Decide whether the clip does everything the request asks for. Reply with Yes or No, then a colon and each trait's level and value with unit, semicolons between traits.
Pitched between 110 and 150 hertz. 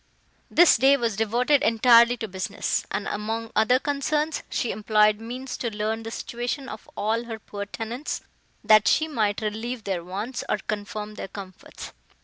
No: high, 225 Hz